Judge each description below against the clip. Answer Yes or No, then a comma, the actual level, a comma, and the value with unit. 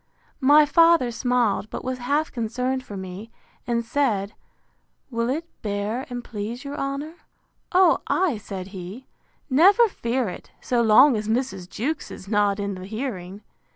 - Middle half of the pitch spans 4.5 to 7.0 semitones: Yes, average, 5.2 semitones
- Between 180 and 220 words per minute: No, average, 150 wpm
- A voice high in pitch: Yes, high, 240 Hz